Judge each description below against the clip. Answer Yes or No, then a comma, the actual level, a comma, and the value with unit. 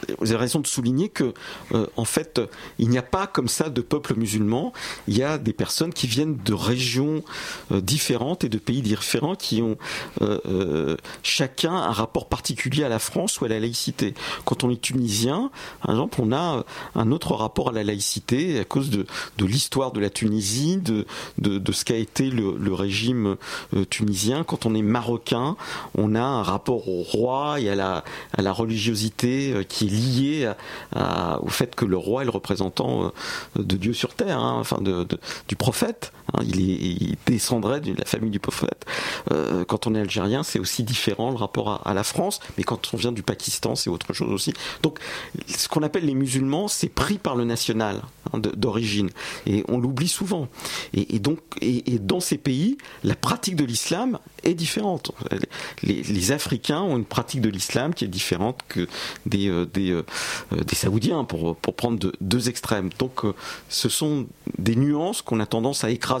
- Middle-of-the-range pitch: No, low, 120 Hz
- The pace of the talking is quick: No, average, 200 wpm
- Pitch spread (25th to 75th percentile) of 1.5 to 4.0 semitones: No, average, 4.5 semitones